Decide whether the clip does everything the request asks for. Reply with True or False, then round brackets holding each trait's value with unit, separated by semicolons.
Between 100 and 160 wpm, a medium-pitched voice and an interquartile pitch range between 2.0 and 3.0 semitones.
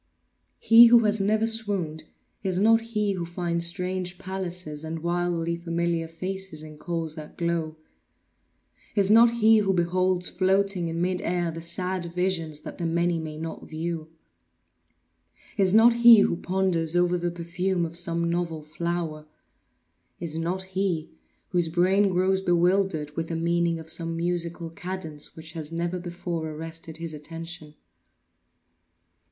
True (145 wpm; 175 Hz; 2.4 semitones)